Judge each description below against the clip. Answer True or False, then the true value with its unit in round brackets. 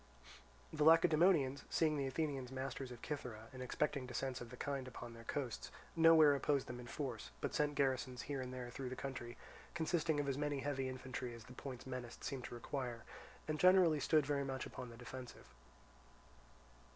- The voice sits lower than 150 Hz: True (135 Hz)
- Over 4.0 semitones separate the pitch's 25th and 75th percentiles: False (2.8 semitones)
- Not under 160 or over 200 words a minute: True (185 wpm)